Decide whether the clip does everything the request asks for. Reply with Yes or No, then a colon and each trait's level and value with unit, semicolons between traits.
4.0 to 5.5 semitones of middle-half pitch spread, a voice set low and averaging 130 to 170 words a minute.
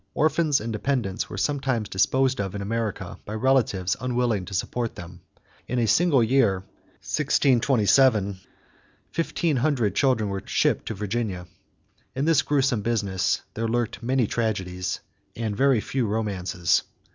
Yes: average, 4.8 semitones; low, 115 Hz; average, 140 wpm